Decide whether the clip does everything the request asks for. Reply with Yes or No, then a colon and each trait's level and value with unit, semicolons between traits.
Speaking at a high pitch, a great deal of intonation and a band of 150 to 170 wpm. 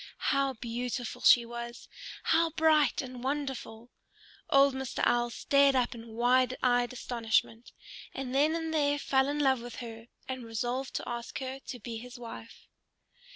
No: very high, 250 Hz; narrow, 2.5 semitones; average, 155 wpm